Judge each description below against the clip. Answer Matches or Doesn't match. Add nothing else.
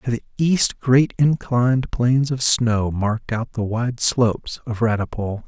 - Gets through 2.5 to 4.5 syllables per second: Matches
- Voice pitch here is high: Doesn't match